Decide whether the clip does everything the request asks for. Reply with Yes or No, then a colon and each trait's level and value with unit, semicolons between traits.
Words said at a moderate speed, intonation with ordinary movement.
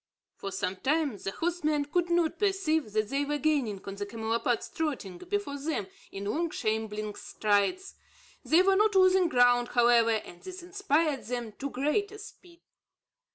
No: average, 155 wpm; wide, 7.9 semitones